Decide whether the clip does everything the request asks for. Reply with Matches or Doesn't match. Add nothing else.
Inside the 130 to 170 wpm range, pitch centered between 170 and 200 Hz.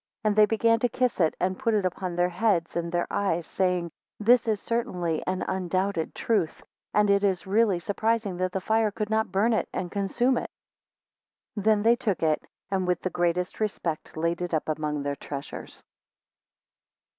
Doesn't match